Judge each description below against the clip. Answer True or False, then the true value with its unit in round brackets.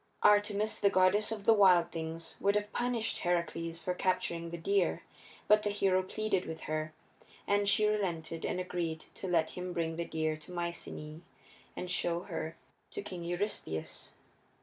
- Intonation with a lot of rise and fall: False (3.4 semitones)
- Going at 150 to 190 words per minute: True (165 wpm)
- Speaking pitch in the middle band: True (180 Hz)